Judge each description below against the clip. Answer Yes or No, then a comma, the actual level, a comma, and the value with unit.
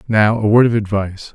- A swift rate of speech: Yes, fast, 225 wpm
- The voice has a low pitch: Yes, low, 105 Hz